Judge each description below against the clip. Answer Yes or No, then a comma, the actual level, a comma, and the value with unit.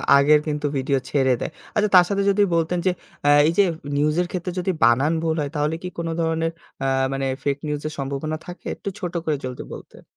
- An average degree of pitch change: Yes, average, 3.7 semitones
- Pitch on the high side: No, medium, 155 Hz